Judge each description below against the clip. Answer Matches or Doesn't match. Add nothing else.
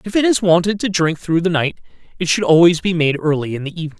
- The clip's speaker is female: Doesn't match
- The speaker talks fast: Matches